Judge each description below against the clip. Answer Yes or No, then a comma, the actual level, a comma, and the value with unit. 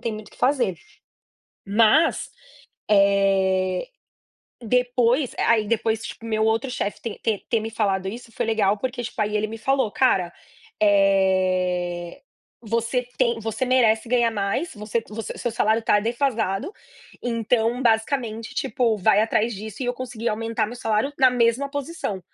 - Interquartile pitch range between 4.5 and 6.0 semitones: No, narrow, 2.6 semitones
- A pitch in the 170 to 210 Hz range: No, high, 225 Hz